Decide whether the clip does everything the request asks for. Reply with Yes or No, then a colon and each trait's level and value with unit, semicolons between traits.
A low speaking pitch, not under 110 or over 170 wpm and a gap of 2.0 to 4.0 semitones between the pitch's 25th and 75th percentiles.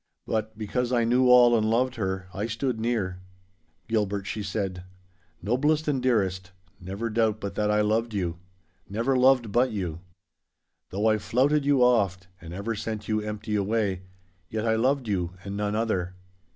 Yes: low, 110 Hz; average, 165 wpm; average, 3.4 semitones